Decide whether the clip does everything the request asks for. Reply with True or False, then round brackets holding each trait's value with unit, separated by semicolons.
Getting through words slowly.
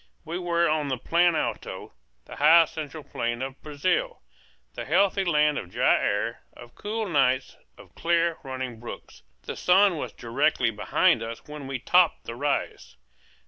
False (160 wpm)